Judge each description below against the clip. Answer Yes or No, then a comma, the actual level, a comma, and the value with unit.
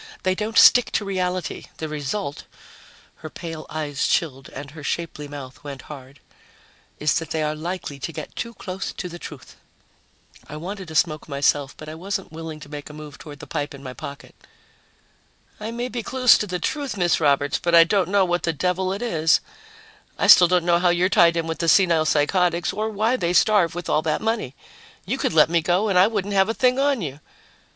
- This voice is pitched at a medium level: Yes, medium, 170 Hz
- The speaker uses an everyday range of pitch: Yes, average, 4.2 semitones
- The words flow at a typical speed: No, fast, 215 wpm